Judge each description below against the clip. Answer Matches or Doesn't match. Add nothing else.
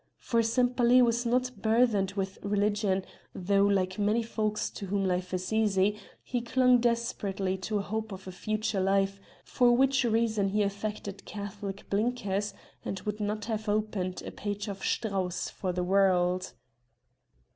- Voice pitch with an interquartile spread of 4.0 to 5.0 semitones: Doesn't match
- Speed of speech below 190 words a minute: Matches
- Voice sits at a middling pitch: Doesn't match